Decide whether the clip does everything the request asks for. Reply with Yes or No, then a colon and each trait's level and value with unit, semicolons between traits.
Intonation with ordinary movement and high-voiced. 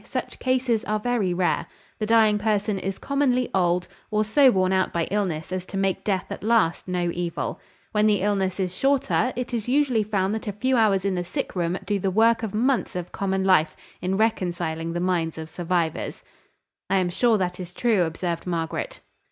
Yes: average, 3.7 semitones; high, 195 Hz